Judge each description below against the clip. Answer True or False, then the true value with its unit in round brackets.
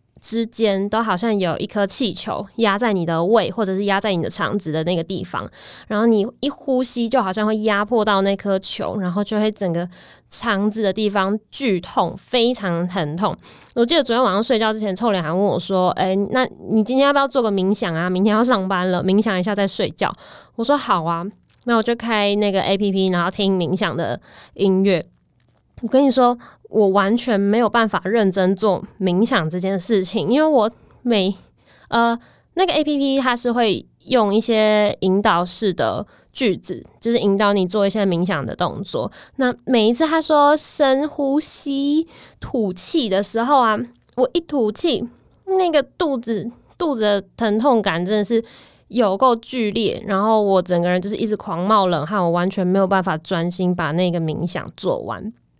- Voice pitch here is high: True (210 Hz)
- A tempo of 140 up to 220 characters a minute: False (270 characters per minute)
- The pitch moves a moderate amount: True (3.8 semitones)